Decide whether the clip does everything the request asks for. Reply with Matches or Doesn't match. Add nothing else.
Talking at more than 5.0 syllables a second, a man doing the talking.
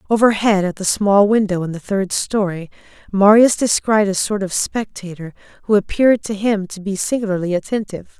Doesn't match